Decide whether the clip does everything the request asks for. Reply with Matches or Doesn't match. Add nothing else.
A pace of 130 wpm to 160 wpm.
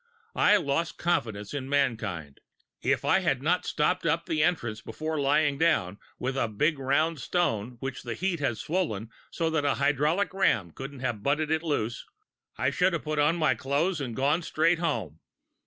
Doesn't match